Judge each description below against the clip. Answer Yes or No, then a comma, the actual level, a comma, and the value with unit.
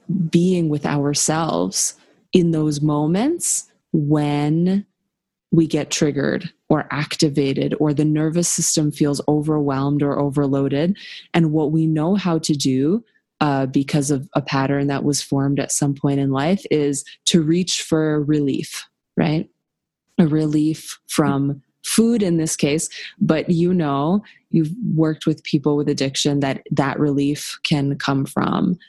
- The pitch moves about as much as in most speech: Yes, average, 3.0 semitones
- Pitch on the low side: No, medium, 155 Hz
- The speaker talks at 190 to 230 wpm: No, average, 140 wpm